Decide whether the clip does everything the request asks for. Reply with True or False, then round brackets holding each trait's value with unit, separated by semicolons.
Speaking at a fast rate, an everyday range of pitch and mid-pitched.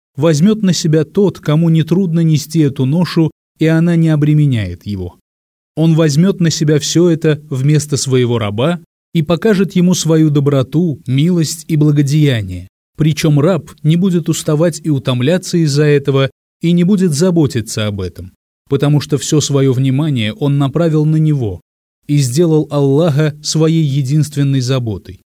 False (145 wpm; 3.5 semitones; 150 Hz)